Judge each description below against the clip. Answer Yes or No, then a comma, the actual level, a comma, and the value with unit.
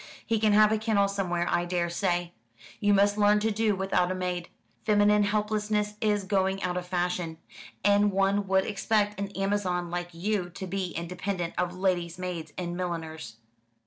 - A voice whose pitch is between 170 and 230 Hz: Yes, high, 190 Hz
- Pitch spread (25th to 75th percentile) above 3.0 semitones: No, average, 2.7 semitones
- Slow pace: No, average, 170 wpm